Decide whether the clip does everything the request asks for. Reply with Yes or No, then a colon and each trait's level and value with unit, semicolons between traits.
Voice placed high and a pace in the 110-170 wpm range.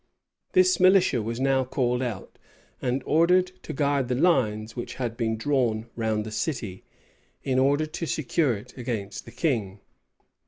No: low, 125 Hz; average, 155 wpm